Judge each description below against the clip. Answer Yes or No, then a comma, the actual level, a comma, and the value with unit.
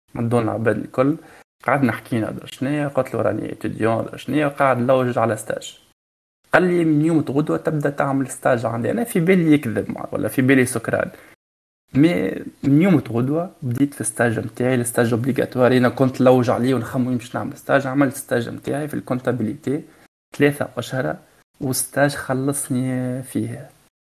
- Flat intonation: No, average, 3.2 semitones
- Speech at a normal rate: No, fast, 150 wpm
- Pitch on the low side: Yes, low, 130 Hz